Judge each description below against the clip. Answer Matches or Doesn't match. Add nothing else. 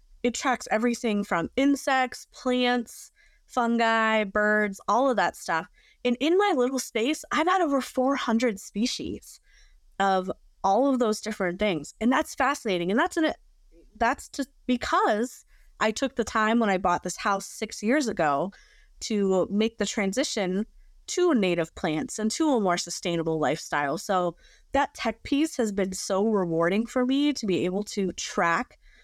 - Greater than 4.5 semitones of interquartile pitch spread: Matches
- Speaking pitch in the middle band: Doesn't match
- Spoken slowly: Doesn't match